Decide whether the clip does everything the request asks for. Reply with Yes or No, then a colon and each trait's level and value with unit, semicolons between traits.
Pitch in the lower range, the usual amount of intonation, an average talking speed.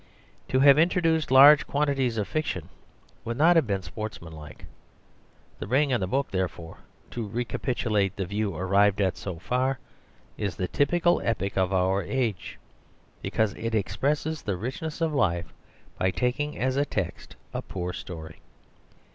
No: low, 110 Hz; wide, 6.9 semitones; average, 155 wpm